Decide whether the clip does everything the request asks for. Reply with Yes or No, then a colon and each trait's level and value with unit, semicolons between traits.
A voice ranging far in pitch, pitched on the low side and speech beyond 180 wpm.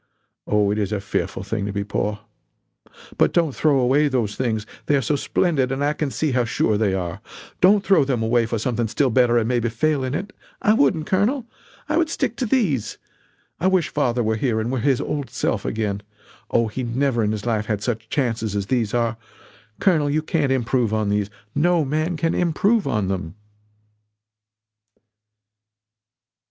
Yes: wide, 5.7 semitones; low, 125 Hz; average, 190 wpm